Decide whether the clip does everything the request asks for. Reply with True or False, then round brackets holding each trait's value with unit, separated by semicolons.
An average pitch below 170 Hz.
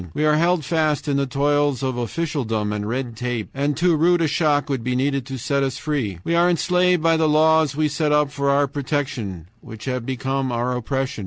True (140 Hz)